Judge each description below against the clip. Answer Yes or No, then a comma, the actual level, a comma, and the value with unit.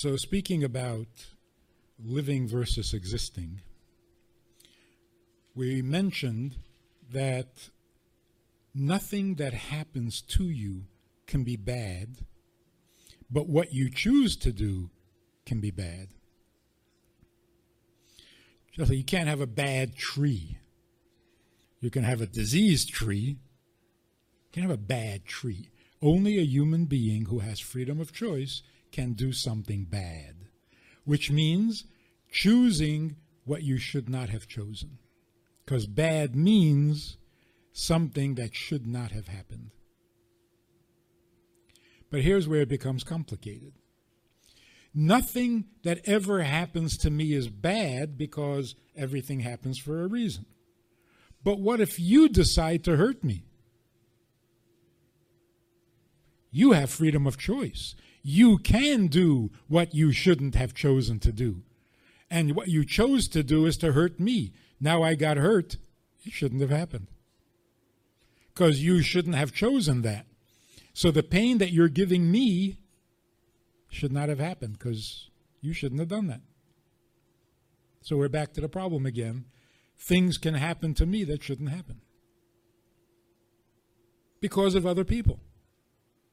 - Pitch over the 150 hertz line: No, low, 135 Hz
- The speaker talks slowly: Yes, slow, 125 wpm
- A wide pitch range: Yes, wide, 6.2 semitones